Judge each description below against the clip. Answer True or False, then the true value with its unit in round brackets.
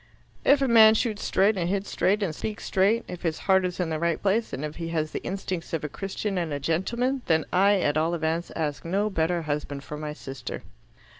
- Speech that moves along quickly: True (225 wpm)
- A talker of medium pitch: True (175 Hz)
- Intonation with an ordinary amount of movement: True (4.2 semitones)